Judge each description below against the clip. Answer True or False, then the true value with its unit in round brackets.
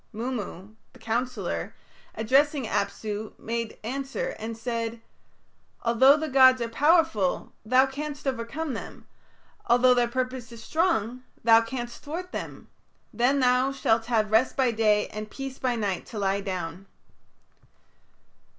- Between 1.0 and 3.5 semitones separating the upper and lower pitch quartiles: True (3.2 semitones)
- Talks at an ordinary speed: False (130 wpm)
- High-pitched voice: True (240 Hz)